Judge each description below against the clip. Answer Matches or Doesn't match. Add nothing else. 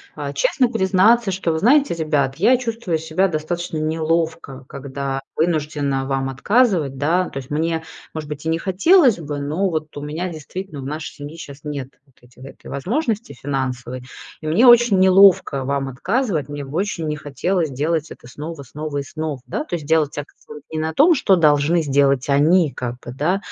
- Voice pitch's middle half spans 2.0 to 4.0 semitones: Doesn't match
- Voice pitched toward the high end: Doesn't match